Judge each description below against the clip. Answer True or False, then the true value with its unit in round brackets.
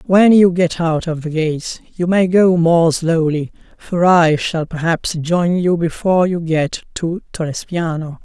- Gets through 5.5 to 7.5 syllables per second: False (4.0 syllables/s)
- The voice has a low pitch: False (170 Hz)